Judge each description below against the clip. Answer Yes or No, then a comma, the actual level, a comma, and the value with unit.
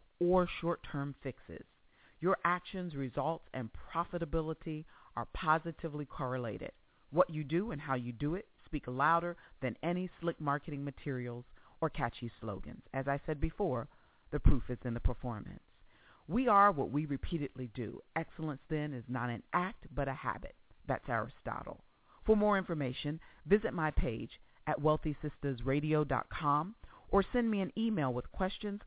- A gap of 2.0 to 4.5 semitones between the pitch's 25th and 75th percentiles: No, average, 4.9 semitones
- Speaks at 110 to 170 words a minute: Yes, average, 150 wpm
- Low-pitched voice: No, medium, 150 Hz